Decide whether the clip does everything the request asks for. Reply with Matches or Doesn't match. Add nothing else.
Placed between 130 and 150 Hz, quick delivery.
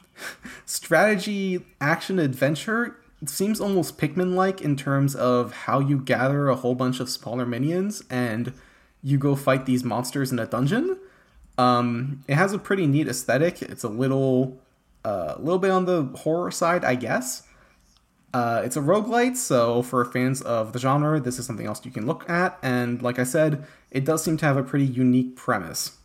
Doesn't match